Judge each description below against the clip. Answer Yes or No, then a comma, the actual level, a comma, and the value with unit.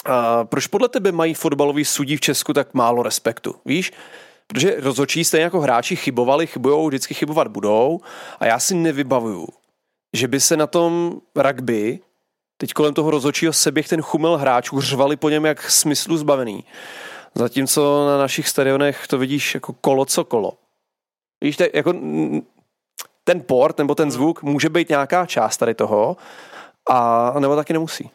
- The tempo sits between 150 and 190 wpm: Yes, average, 160 wpm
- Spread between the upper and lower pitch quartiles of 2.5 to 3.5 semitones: Yes, average, 2.9 semitones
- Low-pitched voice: No, medium, 145 Hz